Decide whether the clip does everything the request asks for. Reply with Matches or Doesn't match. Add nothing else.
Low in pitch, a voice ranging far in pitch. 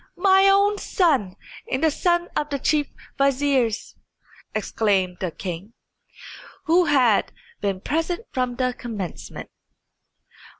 Doesn't match